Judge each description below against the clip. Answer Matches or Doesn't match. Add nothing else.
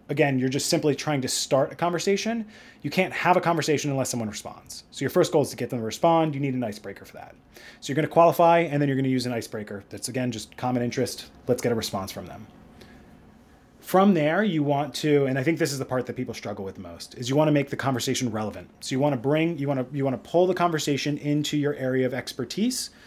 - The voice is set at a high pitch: Doesn't match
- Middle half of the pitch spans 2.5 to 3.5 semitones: Doesn't match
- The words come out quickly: Matches